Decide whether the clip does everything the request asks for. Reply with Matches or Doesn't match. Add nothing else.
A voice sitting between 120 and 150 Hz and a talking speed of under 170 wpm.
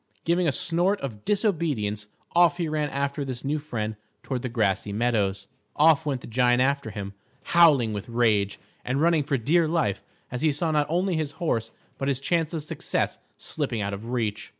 Doesn't match